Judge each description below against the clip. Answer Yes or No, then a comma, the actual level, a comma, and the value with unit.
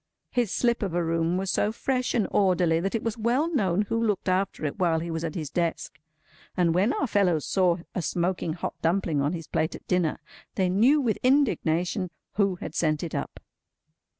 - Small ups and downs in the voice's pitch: No, average, 4.5 semitones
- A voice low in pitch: No, medium, 185 Hz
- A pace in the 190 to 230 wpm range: Yes, fast, 205 wpm